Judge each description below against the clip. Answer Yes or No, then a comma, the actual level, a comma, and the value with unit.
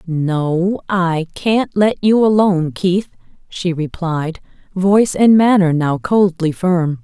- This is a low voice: No, medium, 180 Hz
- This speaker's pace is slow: Yes, slow, 130 wpm